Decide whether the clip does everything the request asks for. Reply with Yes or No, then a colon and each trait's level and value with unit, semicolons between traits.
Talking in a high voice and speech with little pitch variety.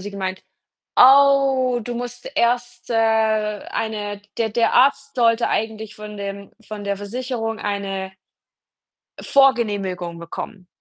No: high, 220 Hz; average, 3.3 semitones